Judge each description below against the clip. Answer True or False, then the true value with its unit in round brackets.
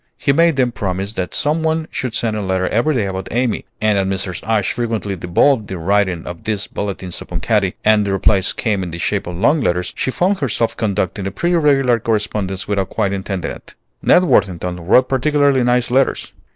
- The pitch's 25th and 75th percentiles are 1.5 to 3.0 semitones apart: False (4.9 semitones)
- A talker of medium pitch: False (105 Hz)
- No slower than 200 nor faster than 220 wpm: True (205 wpm)